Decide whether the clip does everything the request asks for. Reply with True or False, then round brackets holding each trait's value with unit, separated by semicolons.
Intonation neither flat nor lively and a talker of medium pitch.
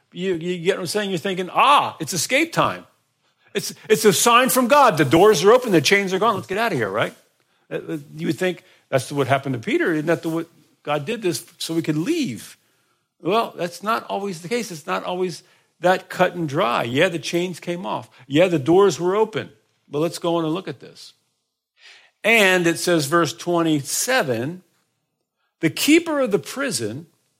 True (3.9 semitones; 175 Hz)